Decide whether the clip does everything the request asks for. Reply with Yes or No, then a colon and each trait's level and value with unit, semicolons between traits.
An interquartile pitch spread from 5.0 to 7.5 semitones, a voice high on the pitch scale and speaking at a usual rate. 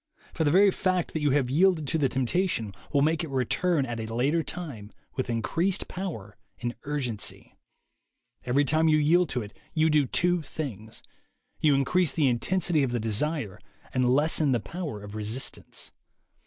No: average, 5.3 semitones; medium, 145 Hz; average, 170 wpm